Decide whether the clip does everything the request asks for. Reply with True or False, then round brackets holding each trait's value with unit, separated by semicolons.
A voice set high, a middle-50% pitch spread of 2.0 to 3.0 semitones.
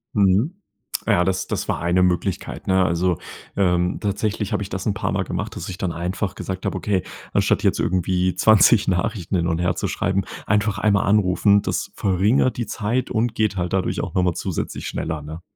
False (95 Hz; 2.5 semitones)